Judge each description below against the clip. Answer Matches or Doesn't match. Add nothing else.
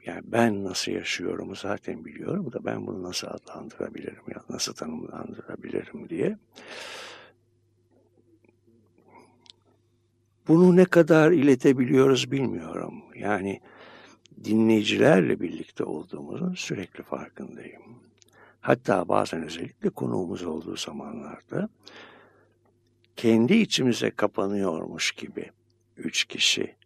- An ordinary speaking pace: Doesn't match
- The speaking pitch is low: Matches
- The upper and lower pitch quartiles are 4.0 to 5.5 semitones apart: Doesn't match